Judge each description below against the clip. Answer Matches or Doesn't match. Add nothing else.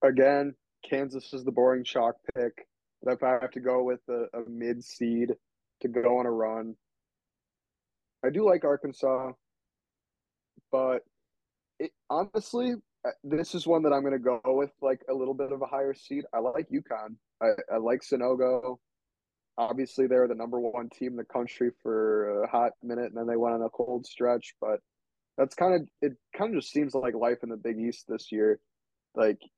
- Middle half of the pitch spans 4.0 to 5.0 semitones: Doesn't match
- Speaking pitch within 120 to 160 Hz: Matches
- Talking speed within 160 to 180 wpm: Doesn't match